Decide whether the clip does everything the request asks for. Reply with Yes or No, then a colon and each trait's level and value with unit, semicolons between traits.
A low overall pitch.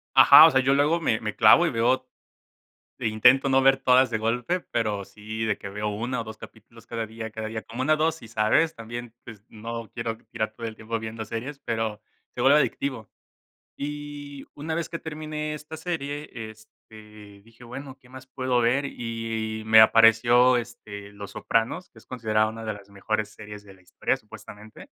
Yes: low, 115 Hz